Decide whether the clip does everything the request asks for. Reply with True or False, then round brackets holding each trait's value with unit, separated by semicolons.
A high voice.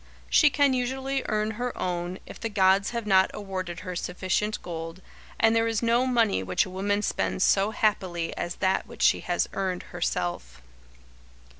True (195 Hz)